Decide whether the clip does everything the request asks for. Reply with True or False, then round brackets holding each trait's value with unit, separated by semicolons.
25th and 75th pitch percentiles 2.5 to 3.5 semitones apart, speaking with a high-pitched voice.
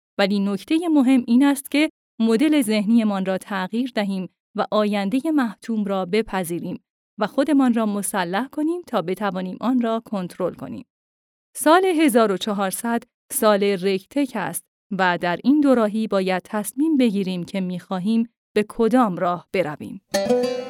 False (4.6 semitones; 215 Hz)